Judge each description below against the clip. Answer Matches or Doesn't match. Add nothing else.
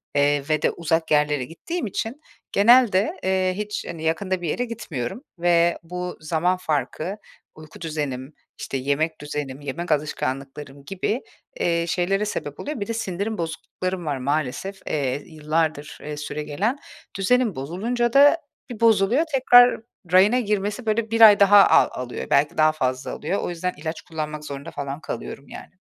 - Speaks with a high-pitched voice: Doesn't match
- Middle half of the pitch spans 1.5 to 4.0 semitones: Doesn't match